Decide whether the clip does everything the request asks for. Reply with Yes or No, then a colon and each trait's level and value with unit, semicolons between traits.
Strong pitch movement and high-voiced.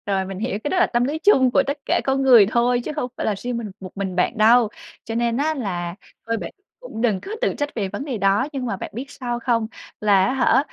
No: average, 4.6 semitones; high, 235 Hz